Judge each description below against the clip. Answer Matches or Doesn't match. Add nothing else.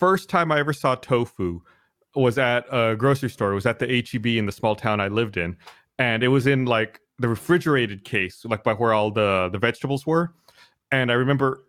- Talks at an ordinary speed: Doesn't match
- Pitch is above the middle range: Doesn't match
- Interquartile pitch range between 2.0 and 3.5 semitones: Doesn't match